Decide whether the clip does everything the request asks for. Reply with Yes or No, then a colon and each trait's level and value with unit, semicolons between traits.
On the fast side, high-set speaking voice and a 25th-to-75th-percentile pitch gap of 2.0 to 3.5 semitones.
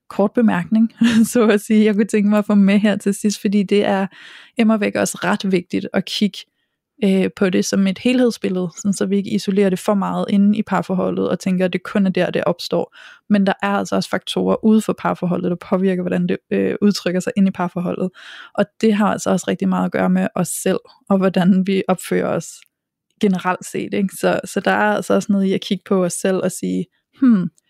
Yes: fast, 230 wpm; high, 195 Hz; narrow, 2.5 semitones